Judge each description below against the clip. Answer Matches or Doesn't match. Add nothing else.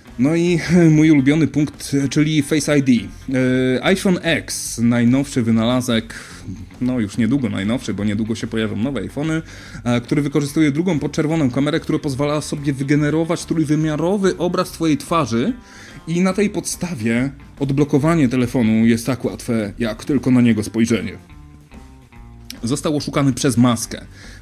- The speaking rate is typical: Matches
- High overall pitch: Doesn't match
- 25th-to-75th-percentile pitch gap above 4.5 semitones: Matches